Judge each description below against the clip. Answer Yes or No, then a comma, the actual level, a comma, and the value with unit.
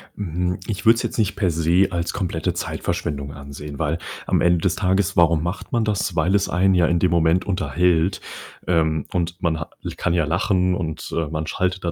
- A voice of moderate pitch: No, very low, 85 Hz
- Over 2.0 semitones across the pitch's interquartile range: Yes, narrow, 2.4 semitones